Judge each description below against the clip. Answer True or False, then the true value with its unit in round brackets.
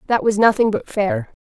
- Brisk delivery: True (210 wpm)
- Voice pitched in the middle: False (220 Hz)